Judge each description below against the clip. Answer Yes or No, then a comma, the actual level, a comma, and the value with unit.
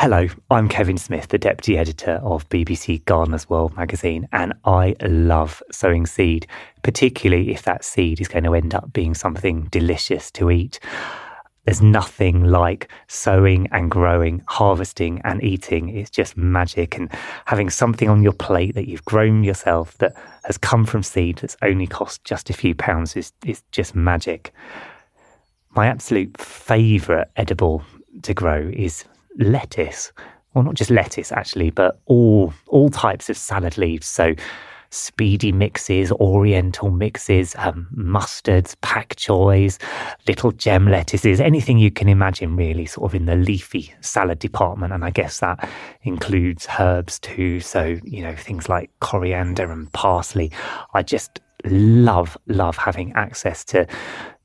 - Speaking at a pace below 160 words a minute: Yes, average, 150 wpm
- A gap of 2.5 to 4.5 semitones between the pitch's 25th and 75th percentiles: Yes, average, 3.4 semitones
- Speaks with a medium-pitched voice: No, very low, 95 Hz